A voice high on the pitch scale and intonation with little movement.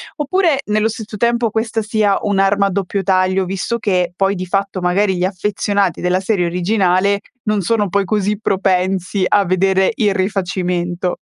Yes: high, 195 Hz; narrow, 2.2 semitones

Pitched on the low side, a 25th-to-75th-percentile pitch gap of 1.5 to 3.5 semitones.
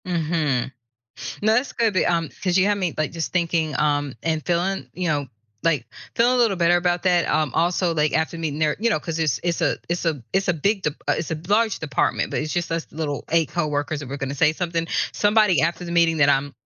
No: medium, 165 Hz; average, 2.9 semitones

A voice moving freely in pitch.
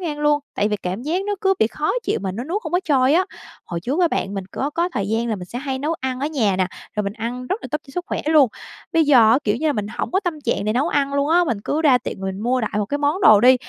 Yes: wide, 6.1 semitones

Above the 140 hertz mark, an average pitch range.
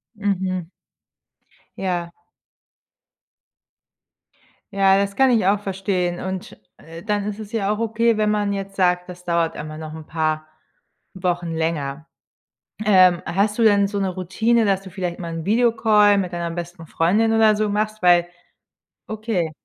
Yes: high, 190 Hz; average, 3.3 semitones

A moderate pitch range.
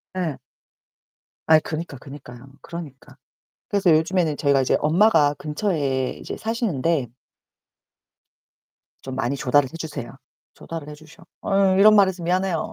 Yes: average, 4.8 semitones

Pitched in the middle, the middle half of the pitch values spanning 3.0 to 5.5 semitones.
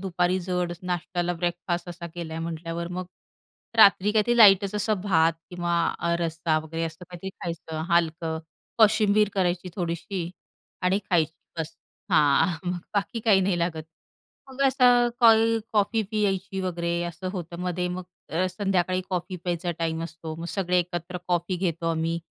No: medium, 175 Hz; narrow, 2.4 semitones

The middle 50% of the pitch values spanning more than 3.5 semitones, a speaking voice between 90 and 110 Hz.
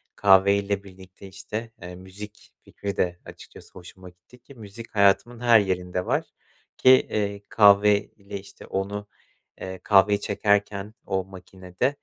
No: narrow, 1.7 semitones; low, 100 Hz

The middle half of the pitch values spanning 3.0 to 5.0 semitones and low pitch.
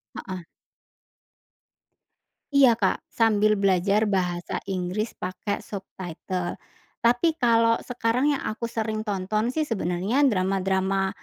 No: average, 3.5 semitones; high, 210 Hz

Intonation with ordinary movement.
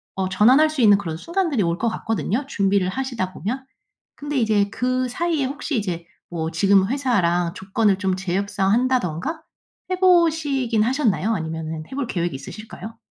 No: wide, 6.1 semitones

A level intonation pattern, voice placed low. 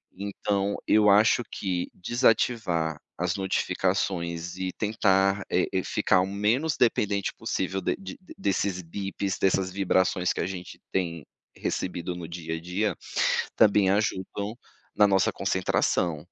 Yes: narrow, 2.3 semitones; very low, 95 Hz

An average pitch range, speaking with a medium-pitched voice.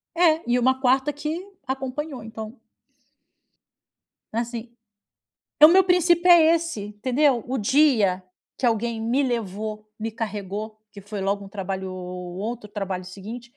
No: average, 4.9 semitones; high, 230 Hz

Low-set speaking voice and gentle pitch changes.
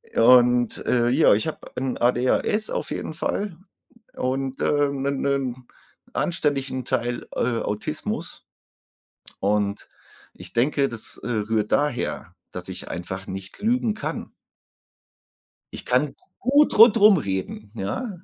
No: low, 130 Hz; average, 4.8 semitones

